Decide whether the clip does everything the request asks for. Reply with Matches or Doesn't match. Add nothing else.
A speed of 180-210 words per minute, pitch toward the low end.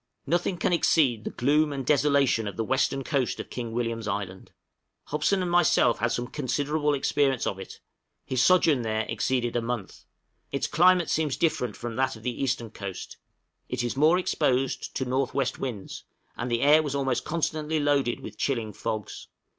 Matches